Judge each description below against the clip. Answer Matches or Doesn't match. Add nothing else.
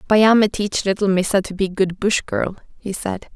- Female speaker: Matches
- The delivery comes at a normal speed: Matches